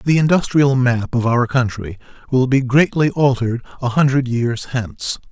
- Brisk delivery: No, average, 160 wpm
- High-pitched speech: No, low, 125 Hz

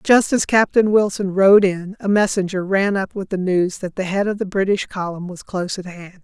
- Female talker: Yes, female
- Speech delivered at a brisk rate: Yes, fast, 230 wpm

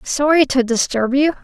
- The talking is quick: No, average, 170 wpm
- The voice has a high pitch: Yes, very high, 270 Hz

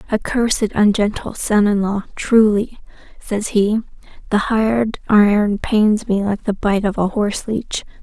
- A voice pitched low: No, high, 210 Hz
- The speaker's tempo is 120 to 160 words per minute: Yes, average, 155 wpm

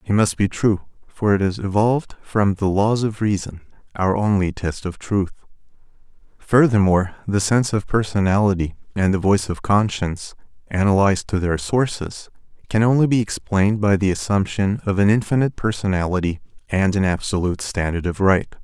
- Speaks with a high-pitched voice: No, low, 100 Hz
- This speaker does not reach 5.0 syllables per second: No, 5.5 syllables/s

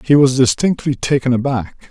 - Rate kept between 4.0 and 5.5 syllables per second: Yes, 5.0 syllables/s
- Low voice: Yes, low, 130 Hz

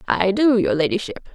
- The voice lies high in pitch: Yes, high, 230 Hz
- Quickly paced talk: No, average, 180 wpm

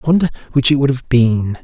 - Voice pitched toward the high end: No, low, 135 Hz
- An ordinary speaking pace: No, fast, 255 wpm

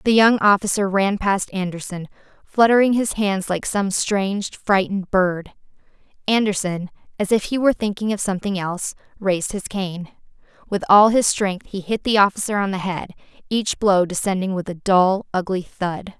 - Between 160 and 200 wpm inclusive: Yes, average, 165 wpm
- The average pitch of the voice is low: No, high, 195 Hz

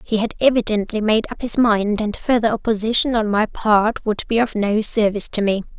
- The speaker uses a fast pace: Yes, fast, 210 wpm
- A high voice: Yes, high, 215 Hz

